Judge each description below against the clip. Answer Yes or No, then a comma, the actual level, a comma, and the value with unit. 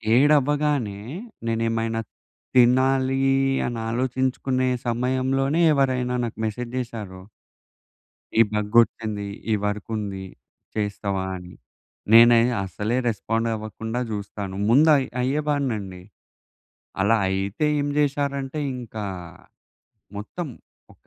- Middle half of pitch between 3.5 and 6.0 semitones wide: Yes, average, 4.0 semitones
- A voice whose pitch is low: Yes, low, 120 Hz